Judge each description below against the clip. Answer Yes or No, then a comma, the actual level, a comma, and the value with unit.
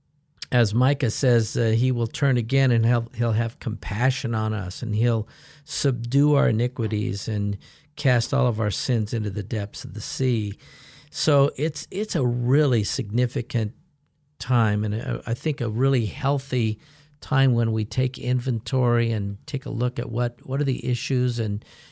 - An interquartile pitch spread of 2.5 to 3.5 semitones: Yes, average, 3.2 semitones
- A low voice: Yes, low, 125 Hz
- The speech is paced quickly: No, average, 165 wpm